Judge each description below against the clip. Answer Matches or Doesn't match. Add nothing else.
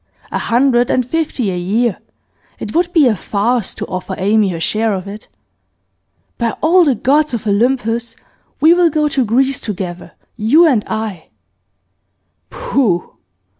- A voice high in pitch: Matches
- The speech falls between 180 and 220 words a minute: Doesn't match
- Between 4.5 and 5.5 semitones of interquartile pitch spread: Matches